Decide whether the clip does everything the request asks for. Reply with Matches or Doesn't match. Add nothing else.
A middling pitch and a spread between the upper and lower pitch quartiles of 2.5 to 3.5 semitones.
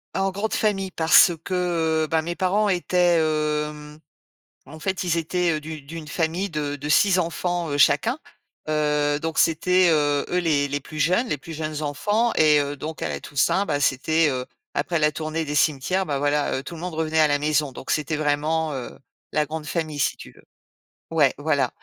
Matches